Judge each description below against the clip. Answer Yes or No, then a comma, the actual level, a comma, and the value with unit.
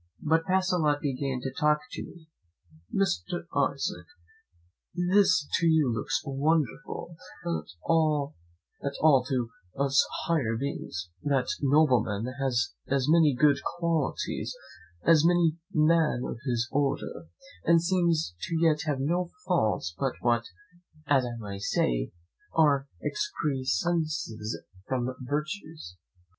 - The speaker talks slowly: Yes, slow, 115 wpm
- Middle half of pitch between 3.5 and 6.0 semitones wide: Yes, average, 4.7 semitones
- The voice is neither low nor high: Yes, medium, 145 Hz